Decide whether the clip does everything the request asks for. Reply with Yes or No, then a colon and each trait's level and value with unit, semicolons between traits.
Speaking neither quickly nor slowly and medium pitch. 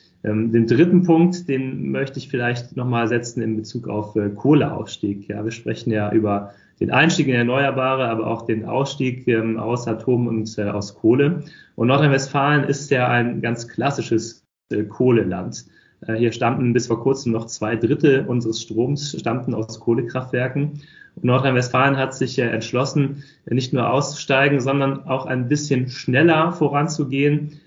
No: average, 160 wpm; low, 125 Hz